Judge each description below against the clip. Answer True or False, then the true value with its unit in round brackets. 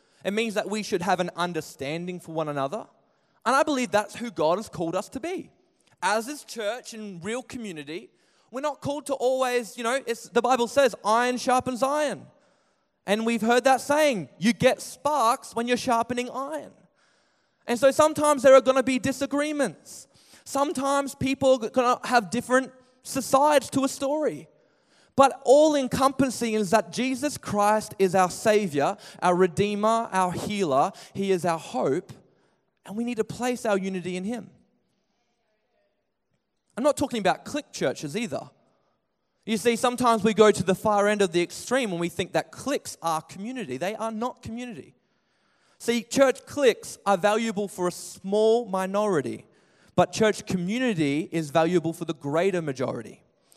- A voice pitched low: False (230 Hz)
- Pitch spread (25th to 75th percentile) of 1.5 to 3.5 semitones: False (5.3 semitones)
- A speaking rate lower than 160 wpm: False (165 wpm)